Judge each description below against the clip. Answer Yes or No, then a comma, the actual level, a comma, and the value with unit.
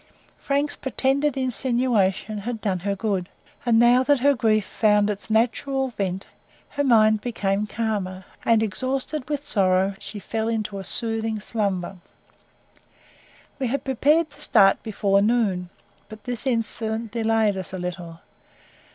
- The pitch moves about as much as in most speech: Yes, average, 4.0 semitones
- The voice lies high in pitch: Yes, high, 220 Hz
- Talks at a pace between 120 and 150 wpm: Yes, average, 140 wpm